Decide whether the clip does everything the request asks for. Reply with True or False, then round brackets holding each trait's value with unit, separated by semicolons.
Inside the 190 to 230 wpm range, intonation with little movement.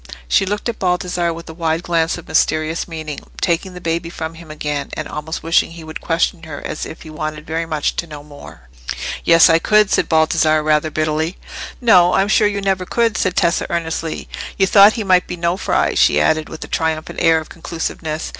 True (205 wpm; 2.3 semitones)